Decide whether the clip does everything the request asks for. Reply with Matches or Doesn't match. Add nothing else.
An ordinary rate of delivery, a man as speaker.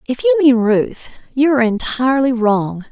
Doesn't match